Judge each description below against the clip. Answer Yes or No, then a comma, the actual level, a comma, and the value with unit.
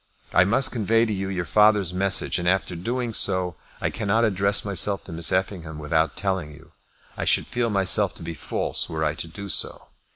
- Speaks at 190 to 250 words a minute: Yes, average, 200 wpm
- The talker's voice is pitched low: Yes, very low, 95 Hz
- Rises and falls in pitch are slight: No, average, 3.6 semitones